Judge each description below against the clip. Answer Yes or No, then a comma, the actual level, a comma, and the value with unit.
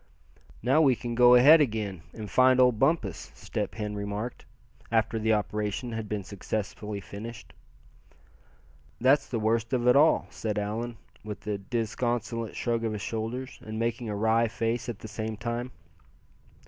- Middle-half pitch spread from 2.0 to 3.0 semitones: Yes, narrow, 2.4 semitones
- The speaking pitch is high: No, low, 115 Hz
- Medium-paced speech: Yes, average, 160 wpm